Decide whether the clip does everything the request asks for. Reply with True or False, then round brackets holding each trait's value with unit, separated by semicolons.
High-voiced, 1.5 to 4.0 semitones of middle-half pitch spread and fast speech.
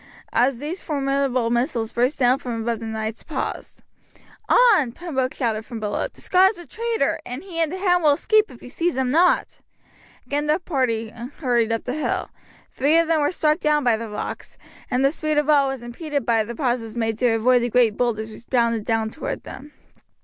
False (255 Hz; 4.7 semitones; 210 wpm)